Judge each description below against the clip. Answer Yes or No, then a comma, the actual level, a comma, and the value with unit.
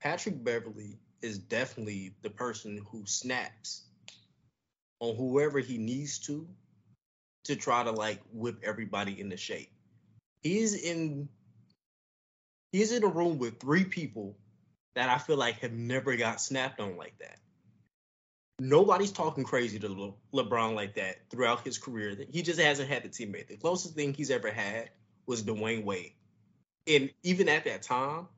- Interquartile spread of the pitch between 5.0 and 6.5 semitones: Yes, average, 5.3 semitones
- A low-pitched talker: Yes, low, 120 Hz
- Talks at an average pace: Yes, average, 150 wpm